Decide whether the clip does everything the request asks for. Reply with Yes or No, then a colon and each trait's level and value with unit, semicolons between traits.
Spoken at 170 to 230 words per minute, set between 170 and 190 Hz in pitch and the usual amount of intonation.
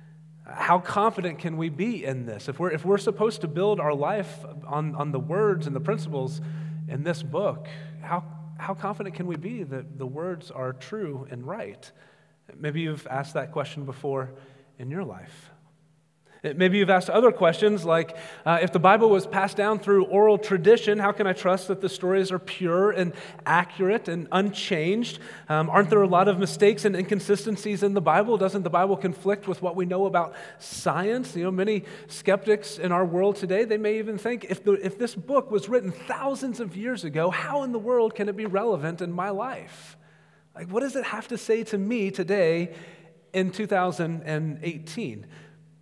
Yes: average, 190 wpm; medium, 185 Hz; average, 4.5 semitones